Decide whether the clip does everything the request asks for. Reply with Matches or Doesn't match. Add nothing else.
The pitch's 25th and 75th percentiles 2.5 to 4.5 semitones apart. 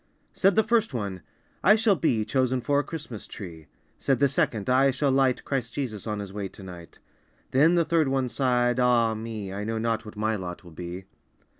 Doesn't match